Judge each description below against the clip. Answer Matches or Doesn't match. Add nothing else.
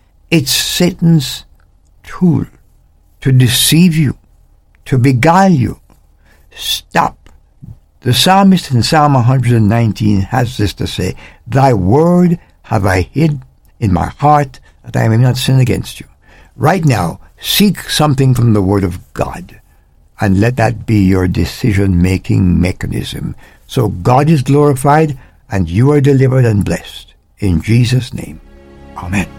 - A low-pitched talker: Matches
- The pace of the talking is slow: Matches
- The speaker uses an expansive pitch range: Matches